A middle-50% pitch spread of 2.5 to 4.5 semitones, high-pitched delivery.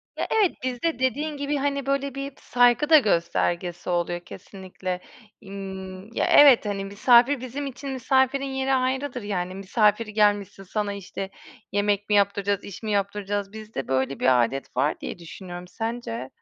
No: wide, 5.6 semitones; high, 205 Hz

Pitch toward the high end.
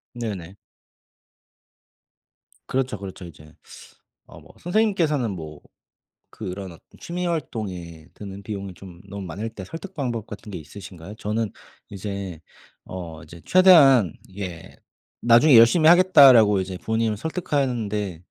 No: low, 105 Hz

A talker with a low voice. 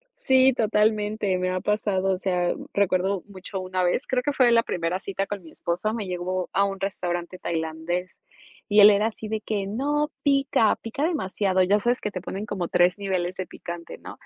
No: high, 195 Hz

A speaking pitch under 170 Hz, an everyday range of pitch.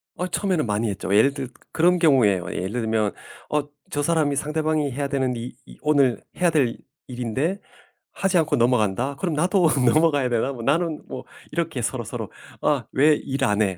Yes: medium, 140 Hz; average, 5.0 semitones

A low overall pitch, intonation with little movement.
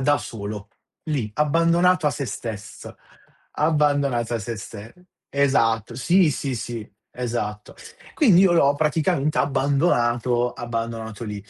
No: low, 125 Hz; average, 4.8 semitones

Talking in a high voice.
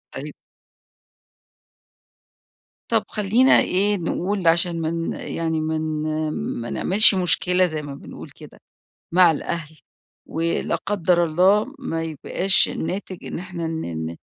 No: medium, 170 Hz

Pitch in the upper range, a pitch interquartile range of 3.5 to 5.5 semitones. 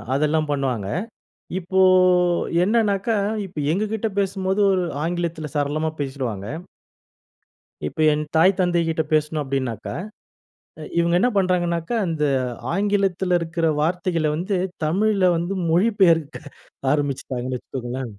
No: medium, 165 Hz; average, 4.4 semitones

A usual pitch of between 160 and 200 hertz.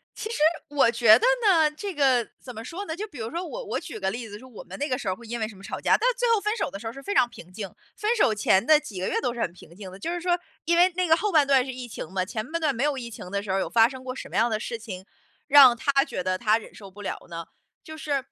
No: very high, 250 Hz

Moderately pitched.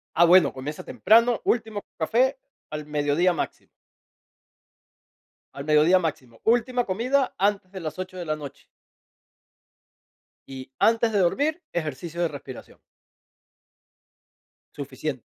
Yes: medium, 180 Hz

